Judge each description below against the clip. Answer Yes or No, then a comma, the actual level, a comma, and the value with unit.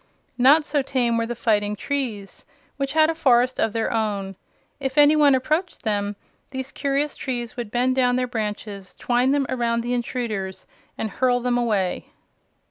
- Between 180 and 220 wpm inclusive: No, average, 170 wpm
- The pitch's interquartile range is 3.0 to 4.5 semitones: Yes, average, 3.5 semitones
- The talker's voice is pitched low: No, high, 245 Hz